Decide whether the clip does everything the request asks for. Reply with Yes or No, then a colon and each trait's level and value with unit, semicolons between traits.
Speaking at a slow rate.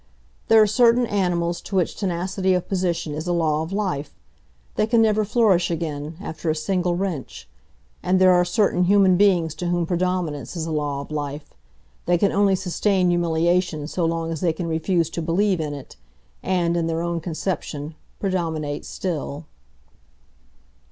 No: average, 165 wpm